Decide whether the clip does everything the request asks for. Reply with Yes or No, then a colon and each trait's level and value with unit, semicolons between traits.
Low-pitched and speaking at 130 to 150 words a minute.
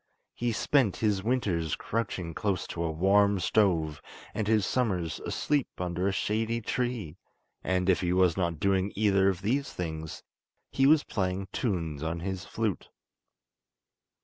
Yes: very low, 95 Hz; average, 145 wpm